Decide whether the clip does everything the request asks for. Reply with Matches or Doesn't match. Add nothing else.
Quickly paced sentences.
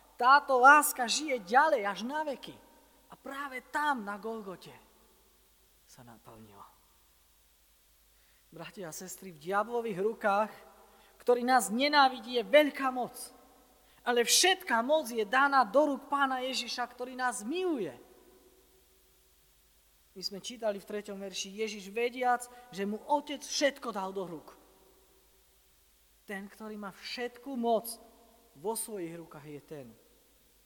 Doesn't match